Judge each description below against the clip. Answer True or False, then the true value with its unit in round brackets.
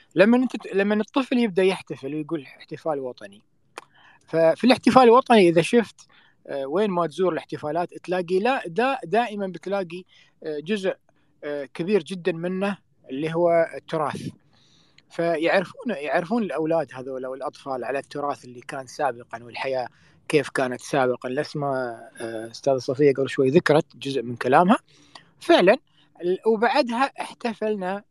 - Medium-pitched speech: True (165 Hz)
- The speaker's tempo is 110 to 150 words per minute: True (120 wpm)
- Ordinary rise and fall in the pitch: False (6.5 semitones)